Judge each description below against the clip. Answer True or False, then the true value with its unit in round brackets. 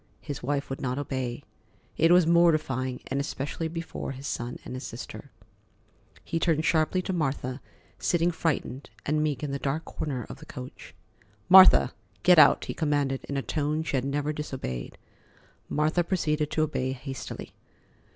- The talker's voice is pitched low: False (145 Hz)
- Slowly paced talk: False (160 wpm)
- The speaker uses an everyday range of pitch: True (3.3 semitones)